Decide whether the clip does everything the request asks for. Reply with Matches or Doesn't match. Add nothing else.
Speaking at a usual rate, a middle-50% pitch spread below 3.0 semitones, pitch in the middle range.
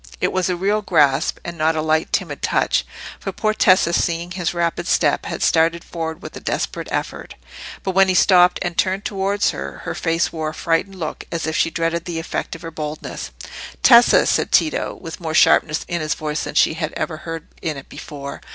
Doesn't match